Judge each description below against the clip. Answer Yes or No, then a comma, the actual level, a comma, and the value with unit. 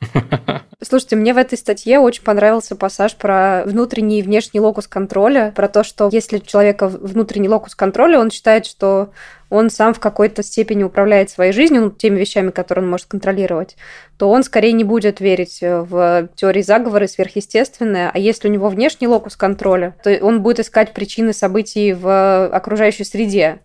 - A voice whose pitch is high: Yes, high, 205 Hz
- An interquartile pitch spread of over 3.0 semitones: No, narrow, 2.4 semitones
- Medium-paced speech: No, fast, 170 wpm